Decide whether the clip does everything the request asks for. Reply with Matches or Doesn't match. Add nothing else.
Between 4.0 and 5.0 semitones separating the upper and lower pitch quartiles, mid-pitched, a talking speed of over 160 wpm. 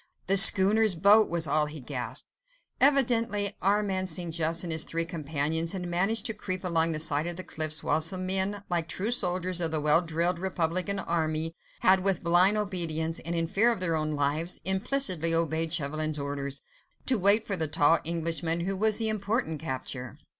Doesn't match